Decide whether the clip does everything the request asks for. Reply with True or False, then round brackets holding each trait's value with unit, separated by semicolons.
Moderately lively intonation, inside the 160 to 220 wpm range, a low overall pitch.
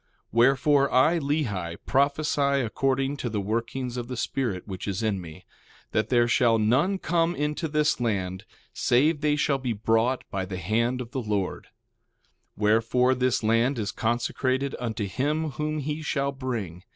True (4.3 semitones; 165 wpm; 125 Hz)